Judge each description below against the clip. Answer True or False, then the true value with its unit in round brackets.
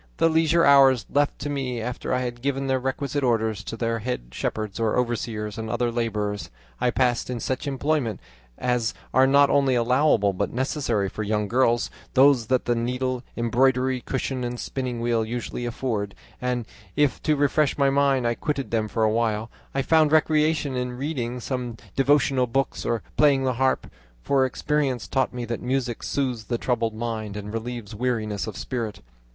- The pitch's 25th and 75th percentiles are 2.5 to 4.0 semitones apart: True (2.9 semitones)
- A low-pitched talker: True (125 Hz)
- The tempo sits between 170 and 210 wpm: True (175 wpm)